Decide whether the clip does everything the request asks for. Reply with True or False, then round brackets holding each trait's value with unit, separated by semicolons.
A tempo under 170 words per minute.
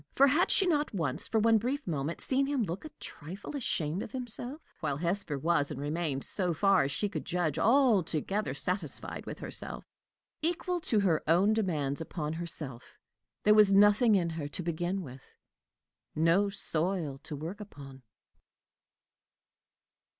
True (155 wpm)